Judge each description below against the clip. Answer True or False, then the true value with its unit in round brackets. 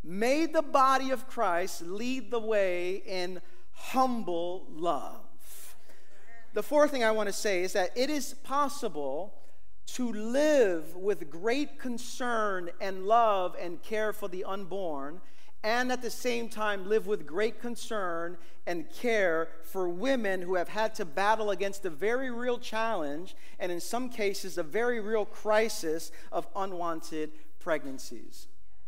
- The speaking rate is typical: True (145 wpm)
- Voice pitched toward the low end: False (210 Hz)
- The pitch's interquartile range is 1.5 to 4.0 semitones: False (5.0 semitones)